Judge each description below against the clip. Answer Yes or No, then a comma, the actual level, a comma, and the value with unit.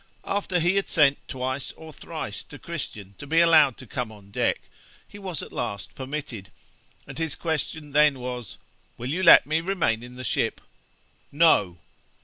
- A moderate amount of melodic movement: Yes, average, 5.0 semitones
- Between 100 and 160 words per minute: No, average, 170 wpm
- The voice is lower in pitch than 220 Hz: Yes, medium, 140 Hz